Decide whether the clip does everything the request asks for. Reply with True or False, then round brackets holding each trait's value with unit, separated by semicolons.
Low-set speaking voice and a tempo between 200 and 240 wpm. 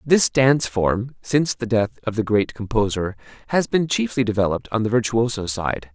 False (115 Hz; 180 wpm)